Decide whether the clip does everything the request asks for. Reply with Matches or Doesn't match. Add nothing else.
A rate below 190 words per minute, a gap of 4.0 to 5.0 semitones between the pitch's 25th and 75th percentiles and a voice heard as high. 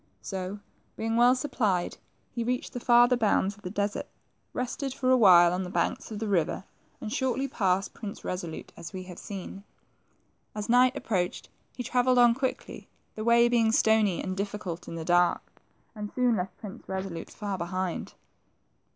Matches